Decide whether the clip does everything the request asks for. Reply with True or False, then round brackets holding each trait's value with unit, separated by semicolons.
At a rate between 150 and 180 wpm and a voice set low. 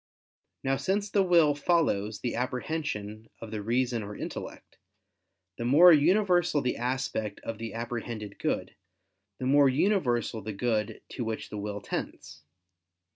False (140 wpm; 125 Hz)